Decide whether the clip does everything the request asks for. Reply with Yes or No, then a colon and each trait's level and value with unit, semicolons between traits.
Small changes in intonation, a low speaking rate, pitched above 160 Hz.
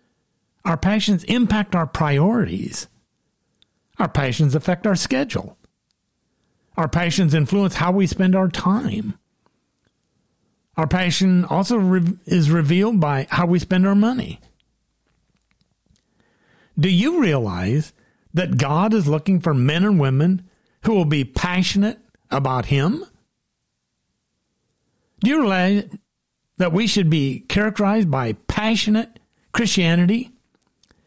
No: average, 4.5 semitones; slow, 110 wpm; medium, 185 Hz